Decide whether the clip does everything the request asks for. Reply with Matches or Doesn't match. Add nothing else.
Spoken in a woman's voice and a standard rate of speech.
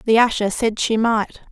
Matches